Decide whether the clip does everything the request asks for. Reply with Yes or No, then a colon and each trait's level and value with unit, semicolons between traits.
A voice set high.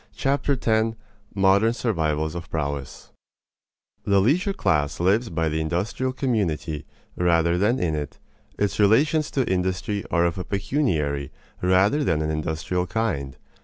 No: very low, 95 Hz